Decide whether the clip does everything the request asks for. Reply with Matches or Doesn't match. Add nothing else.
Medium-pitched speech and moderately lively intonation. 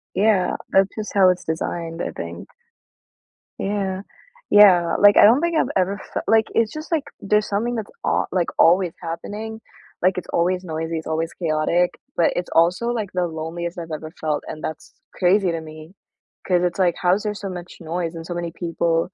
Matches